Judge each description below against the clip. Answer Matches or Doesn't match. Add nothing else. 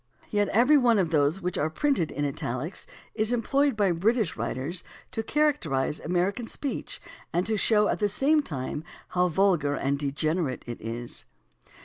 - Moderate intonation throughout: Doesn't match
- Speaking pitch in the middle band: Matches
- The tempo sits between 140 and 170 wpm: Matches